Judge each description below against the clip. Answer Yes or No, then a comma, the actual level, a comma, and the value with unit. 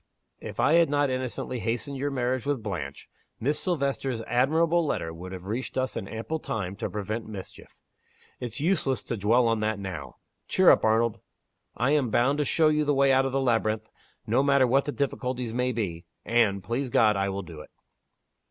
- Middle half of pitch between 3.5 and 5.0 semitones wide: Yes, average, 4.4 semitones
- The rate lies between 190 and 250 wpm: Yes, average, 195 wpm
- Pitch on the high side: No, low, 120 Hz